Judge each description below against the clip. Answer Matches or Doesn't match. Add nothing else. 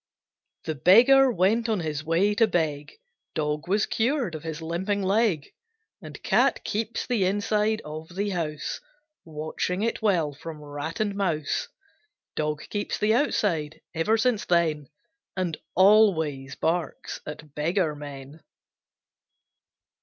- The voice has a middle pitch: Matches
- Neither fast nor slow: Doesn't match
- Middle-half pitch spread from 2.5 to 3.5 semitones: Doesn't match